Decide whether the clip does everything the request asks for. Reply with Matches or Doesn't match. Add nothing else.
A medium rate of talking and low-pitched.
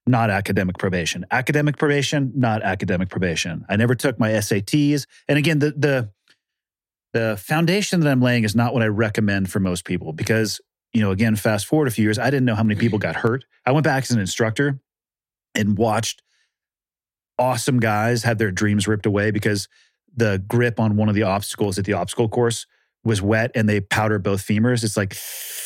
Matches